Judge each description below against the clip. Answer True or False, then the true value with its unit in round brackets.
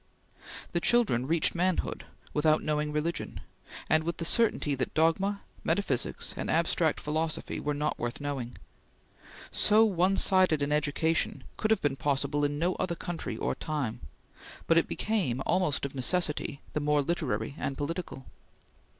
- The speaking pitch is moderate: True (155 Hz)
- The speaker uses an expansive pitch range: False (3.4 semitones)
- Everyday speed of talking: True (150 wpm)